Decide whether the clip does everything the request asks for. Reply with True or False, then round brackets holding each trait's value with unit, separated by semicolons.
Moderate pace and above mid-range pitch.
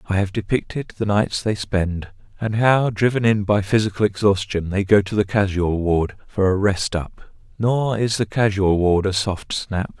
False (190 wpm; 100 Hz)